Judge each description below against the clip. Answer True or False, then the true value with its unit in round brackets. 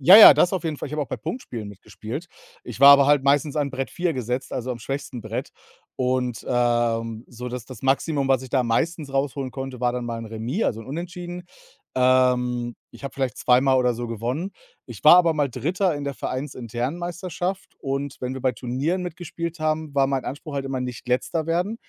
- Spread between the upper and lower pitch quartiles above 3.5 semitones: True (4.0 semitones)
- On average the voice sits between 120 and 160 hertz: True (135 Hz)